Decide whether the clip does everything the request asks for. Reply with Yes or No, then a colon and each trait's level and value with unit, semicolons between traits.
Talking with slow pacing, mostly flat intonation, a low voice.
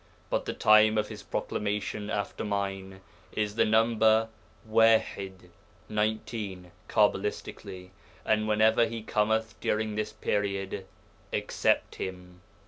Yes: slow, 110 wpm; narrow, 2.0 semitones; low, 105 Hz